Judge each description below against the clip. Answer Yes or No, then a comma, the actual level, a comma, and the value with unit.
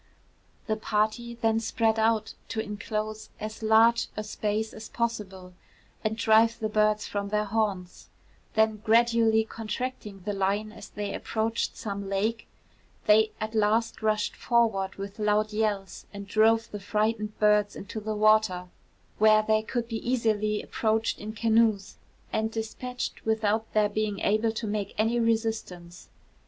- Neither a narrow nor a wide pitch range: No, narrow, 1.2 semitones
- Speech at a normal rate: Yes, average, 145 wpm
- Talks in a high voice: Yes, high, 215 Hz